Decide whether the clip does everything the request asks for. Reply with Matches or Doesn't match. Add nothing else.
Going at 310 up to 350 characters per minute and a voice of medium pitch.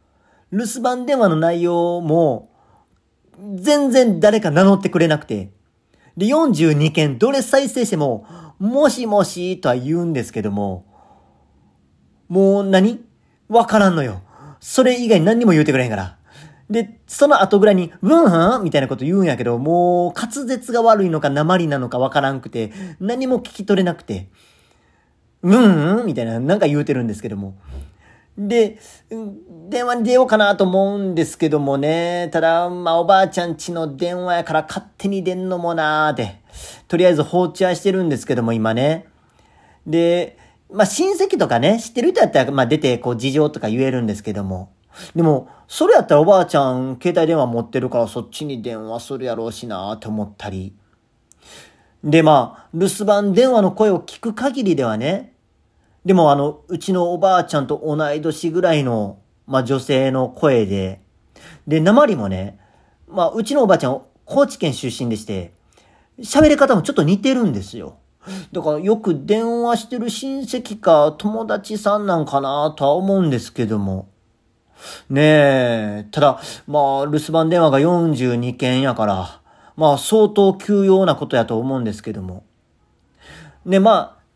Matches